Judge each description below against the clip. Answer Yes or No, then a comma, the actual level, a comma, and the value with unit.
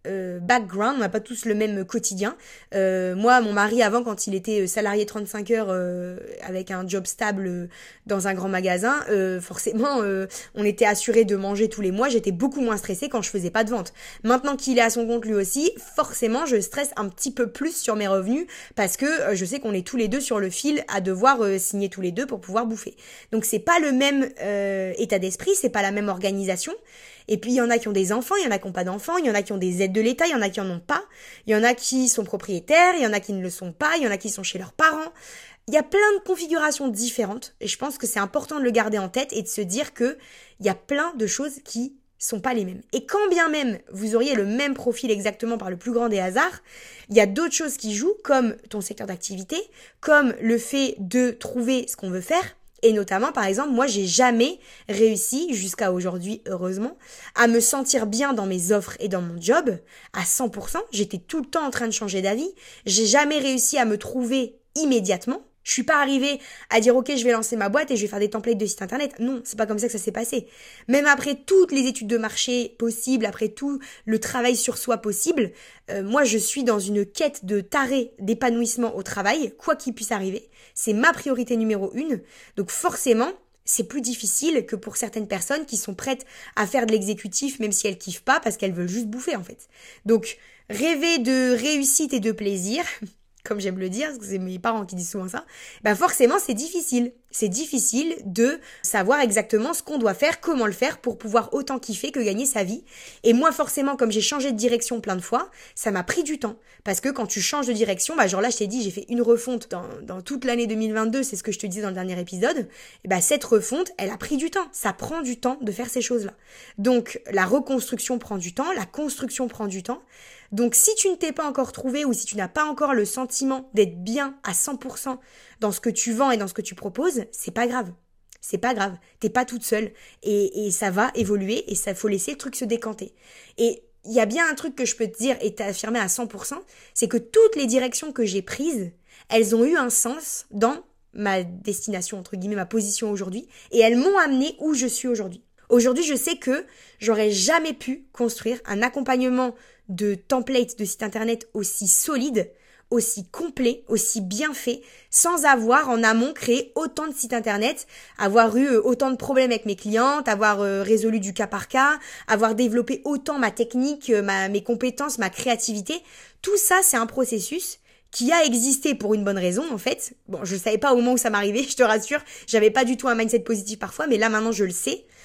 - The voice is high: Yes, high, 230 Hz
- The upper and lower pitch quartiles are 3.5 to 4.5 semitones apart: Yes, average, 4.2 semitones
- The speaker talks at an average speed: No, fast, 235 wpm